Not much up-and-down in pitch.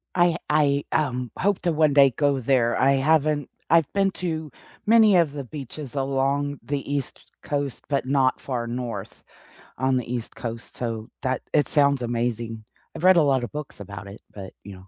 No: average, 3.6 semitones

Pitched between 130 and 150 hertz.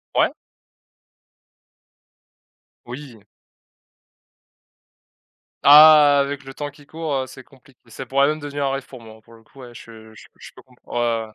Yes: low, 135 Hz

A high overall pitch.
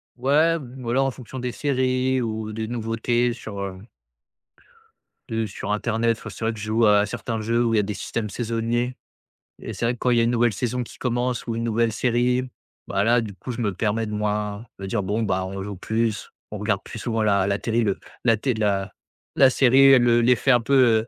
No: low, 115 Hz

